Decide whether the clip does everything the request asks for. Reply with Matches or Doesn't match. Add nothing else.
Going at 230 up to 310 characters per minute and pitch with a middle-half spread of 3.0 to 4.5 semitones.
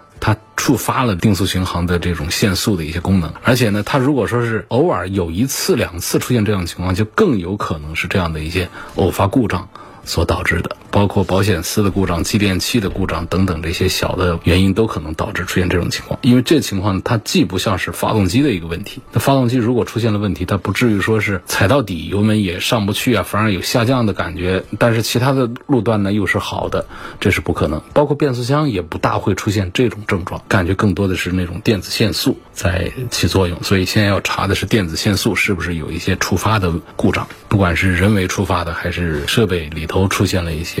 Doesn't match